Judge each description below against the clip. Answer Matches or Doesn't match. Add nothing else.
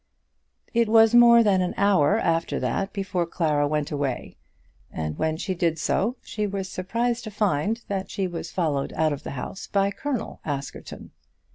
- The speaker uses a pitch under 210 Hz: Matches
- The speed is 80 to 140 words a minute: Doesn't match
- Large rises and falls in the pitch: Matches